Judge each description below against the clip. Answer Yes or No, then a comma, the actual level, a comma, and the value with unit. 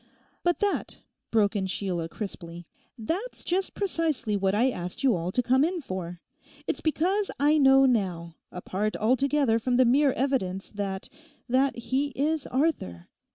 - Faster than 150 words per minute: No, average, 145 wpm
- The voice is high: Yes, very high, 250 Hz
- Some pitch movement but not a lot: No, wide, 7.3 semitones